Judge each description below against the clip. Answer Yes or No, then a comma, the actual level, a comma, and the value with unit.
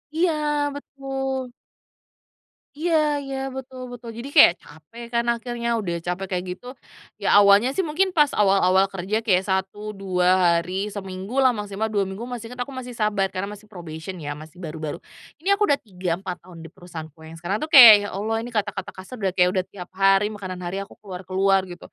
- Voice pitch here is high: Yes, high, 200 Hz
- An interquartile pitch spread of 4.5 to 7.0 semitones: Yes, average, 4.9 semitones